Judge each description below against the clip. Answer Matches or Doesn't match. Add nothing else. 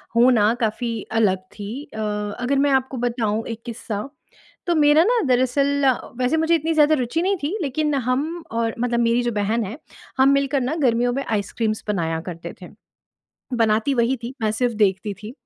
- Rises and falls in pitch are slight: Doesn't match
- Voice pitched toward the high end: Matches